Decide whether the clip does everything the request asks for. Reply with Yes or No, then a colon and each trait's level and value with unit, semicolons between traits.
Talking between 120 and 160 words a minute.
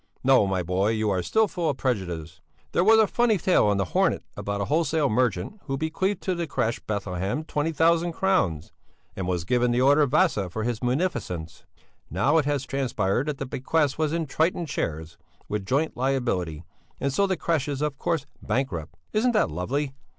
No: average, 195 wpm